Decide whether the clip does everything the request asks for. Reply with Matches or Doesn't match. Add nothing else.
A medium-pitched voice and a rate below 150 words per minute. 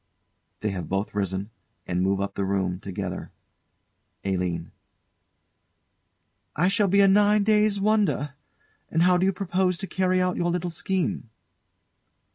Matches